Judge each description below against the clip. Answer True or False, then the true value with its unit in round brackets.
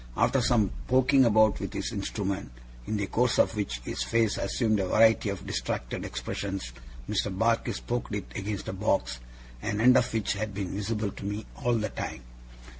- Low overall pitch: True (105 Hz)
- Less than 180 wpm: False (185 wpm)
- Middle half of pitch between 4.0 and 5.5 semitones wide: False (2.6 semitones)